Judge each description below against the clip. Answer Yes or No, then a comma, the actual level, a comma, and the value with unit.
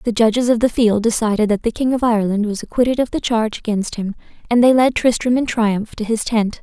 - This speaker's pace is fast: Yes, fast, 245 wpm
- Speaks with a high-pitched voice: Yes, high, 225 Hz